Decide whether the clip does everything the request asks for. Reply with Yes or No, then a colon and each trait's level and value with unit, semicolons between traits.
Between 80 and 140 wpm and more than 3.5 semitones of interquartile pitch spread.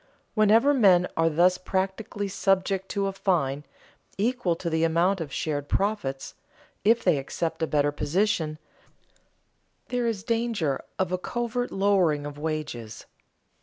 Yes: slow, 135 wpm; average, 4.8 semitones